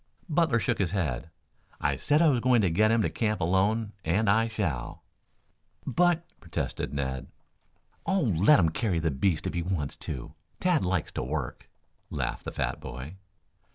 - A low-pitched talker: Yes, very low, 95 Hz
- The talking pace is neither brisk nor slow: Yes, average, 175 wpm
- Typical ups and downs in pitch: No, wide, 6.3 semitones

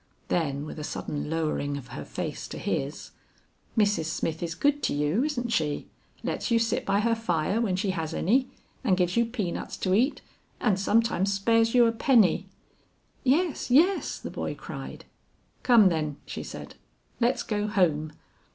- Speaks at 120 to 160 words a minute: No, average, 170 wpm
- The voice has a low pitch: No, high, 200 Hz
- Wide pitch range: Yes, wide, 6.2 semitones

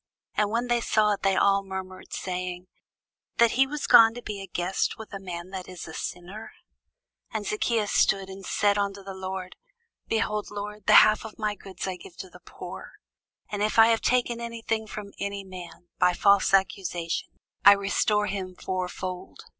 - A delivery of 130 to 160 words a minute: No, average, 185 wpm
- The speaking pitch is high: Yes, high, 200 Hz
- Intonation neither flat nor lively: No, narrow, 2.3 semitones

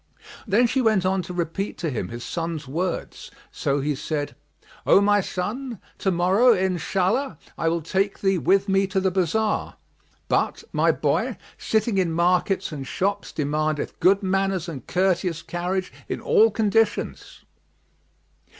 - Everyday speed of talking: Yes, average, 150 wpm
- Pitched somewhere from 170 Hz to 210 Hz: Yes, medium, 185 Hz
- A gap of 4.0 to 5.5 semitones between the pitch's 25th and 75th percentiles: No, average, 3.1 semitones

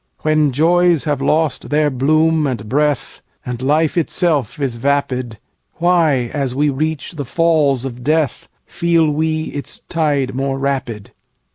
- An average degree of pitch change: Yes, average, 3.1 semitones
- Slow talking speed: Yes, slow, 125 wpm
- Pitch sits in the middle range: Yes, medium, 145 Hz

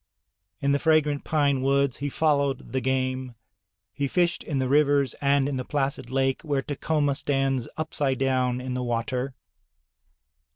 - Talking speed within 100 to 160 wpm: Yes, average, 155 wpm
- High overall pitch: No, low, 135 Hz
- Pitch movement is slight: Yes, narrow, 1.7 semitones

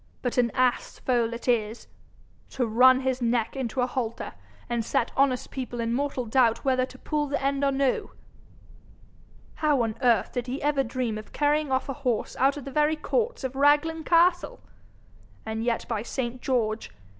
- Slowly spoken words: No, average, 180 wpm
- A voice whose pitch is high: Yes, very high, 255 Hz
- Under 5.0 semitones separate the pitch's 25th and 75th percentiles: Yes, average, 2.9 semitones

